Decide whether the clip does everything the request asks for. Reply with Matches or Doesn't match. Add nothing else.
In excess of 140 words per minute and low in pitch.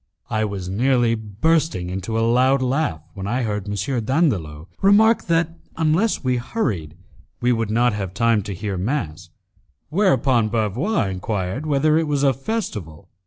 Matches